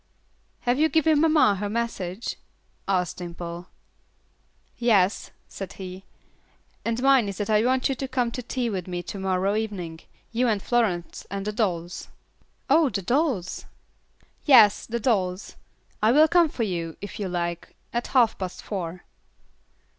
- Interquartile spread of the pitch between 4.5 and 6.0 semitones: Yes, average, 5.0 semitones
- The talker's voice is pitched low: No, high, 210 Hz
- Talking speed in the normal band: Yes, average, 155 wpm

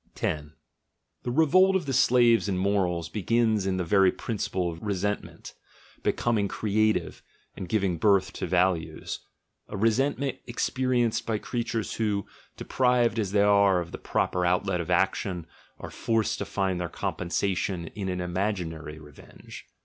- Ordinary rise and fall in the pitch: Yes, average, 4.1 semitones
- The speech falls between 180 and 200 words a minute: No, average, 150 wpm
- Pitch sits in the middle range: No, low, 100 Hz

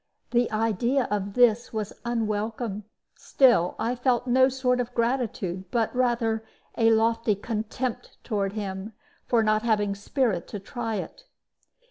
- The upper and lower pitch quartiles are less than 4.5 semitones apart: Yes, average, 2.7 semitones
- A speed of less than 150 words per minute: Yes, slow, 135 wpm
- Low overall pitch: No, high, 225 Hz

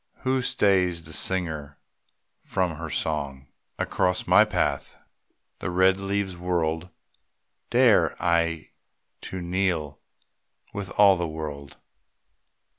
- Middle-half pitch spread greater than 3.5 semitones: No, average, 3.2 semitones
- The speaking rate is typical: No, slow, 105 wpm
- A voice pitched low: Yes, very low, 90 Hz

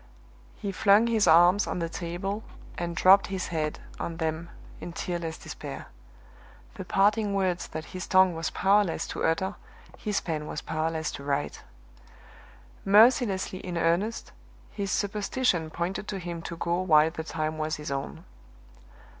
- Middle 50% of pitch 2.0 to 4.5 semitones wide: Yes, average, 3.4 semitones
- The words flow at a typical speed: Yes, average, 150 wpm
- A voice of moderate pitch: Yes, medium, 175 Hz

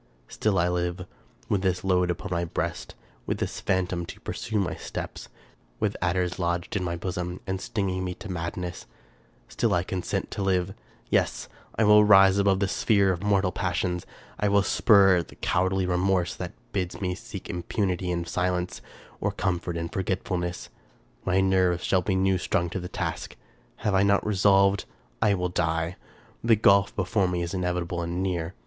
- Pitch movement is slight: Yes, narrow, 1.7 semitones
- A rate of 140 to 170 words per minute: No, average, 180 wpm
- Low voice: Yes, very low, 90 Hz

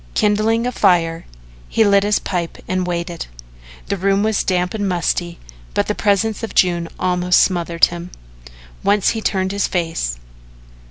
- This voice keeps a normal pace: Yes, average, 155 wpm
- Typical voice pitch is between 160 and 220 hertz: Yes, medium, 185 Hz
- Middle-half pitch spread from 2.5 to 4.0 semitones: Yes, average, 2.9 semitones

